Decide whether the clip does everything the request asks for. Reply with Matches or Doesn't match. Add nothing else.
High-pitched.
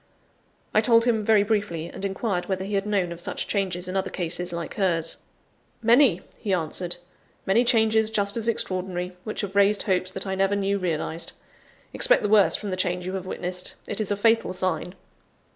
Matches